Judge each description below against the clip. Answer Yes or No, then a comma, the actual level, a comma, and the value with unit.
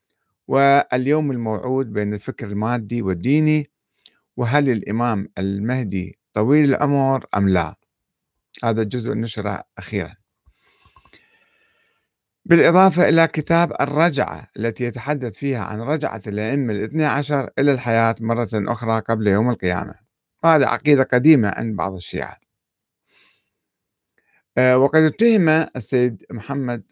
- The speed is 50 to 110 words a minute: Yes, average, 105 wpm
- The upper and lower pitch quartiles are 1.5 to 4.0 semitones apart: No, wide, 5.4 semitones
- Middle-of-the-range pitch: No, low, 120 Hz